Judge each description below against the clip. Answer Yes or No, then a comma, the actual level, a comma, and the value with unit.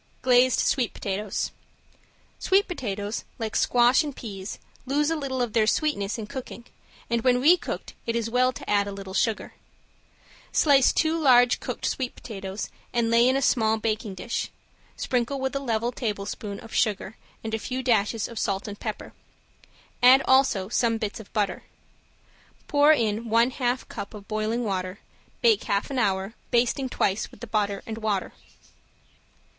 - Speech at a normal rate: Yes, average, 165 wpm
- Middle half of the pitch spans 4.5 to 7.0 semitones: No, average, 3.6 semitones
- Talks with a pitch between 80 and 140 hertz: No, high, 230 Hz